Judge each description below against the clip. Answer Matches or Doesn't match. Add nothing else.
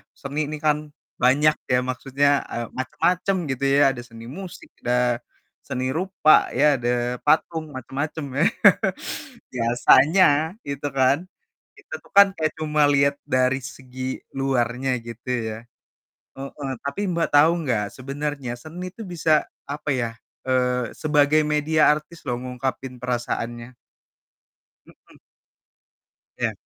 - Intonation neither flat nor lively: Matches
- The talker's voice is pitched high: Doesn't match